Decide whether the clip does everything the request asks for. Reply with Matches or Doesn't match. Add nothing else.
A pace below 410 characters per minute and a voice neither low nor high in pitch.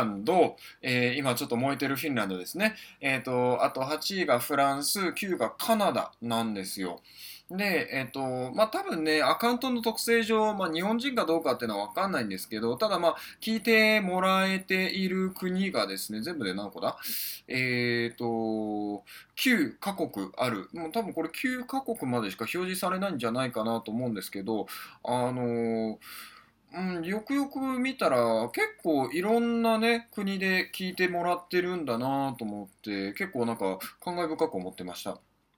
Matches